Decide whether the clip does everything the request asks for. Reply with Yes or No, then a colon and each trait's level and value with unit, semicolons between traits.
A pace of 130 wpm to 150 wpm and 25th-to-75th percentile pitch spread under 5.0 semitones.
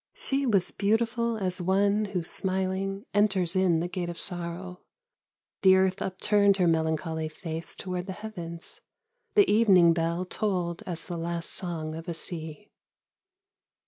Yes: average, 145 wpm; average, 2.9 semitones